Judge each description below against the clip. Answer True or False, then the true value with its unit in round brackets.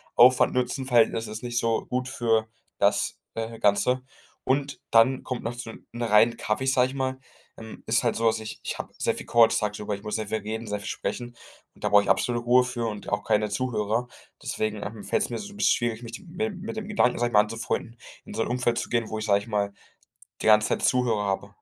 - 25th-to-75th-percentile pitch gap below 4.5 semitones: True (2.6 semitones)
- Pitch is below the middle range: True (115 Hz)